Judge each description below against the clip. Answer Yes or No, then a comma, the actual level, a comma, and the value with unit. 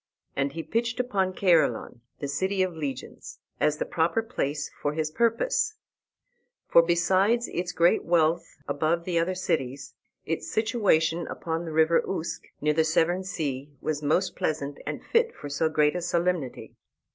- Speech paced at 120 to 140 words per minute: No, average, 155 wpm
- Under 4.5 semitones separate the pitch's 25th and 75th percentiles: Yes, average, 3.6 semitones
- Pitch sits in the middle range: Yes, medium, 165 Hz